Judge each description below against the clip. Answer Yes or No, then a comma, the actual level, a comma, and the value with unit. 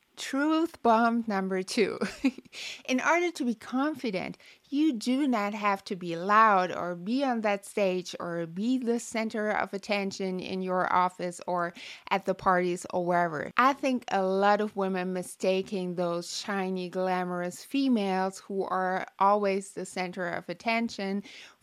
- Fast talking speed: No, average, 150 wpm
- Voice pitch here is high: Yes, high, 195 Hz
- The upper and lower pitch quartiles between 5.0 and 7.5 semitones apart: No, average, 4.3 semitones